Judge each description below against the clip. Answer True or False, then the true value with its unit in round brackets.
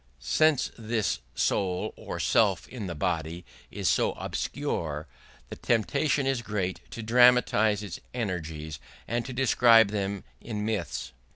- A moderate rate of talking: False (130 wpm)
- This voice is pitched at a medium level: False (105 Hz)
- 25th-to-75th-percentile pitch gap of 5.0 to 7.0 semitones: True (5.4 semitones)